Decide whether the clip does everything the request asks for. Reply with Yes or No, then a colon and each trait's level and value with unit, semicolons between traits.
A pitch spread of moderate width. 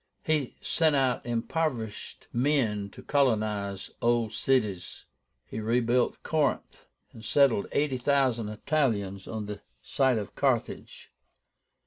Yes: average, 4.5 semitones